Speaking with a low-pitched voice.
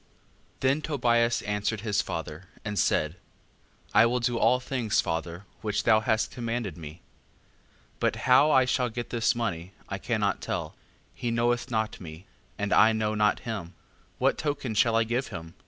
Yes: low, 115 Hz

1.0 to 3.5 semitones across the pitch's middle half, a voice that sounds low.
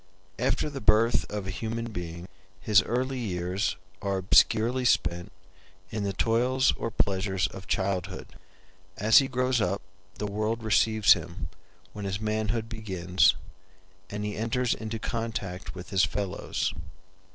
Yes: average, 3.2 semitones; low, 105 Hz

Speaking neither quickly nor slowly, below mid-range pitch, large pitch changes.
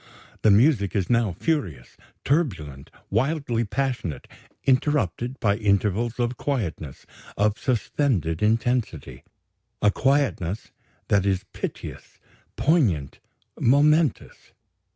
No: slow, 90 wpm; low, 115 Hz; wide, 5.8 semitones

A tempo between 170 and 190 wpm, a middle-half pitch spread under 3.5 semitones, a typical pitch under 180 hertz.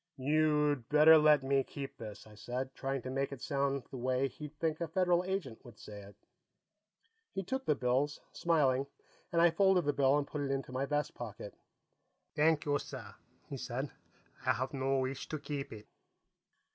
Yes: average, 185 wpm; average, 2.8 semitones; medium, 140 Hz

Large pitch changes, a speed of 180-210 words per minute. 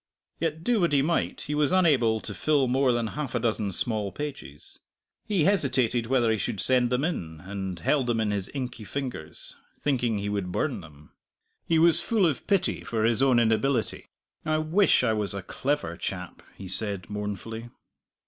Yes: wide, 6.1 semitones; average, 185 wpm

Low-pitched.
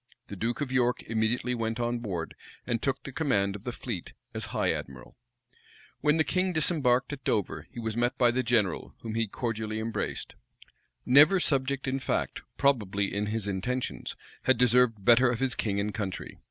Yes: low, 120 Hz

